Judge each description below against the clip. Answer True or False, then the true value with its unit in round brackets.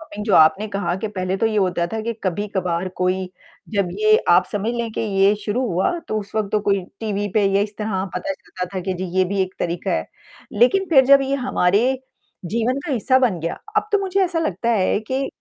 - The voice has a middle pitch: False (205 Hz)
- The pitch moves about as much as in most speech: True (4.4 semitones)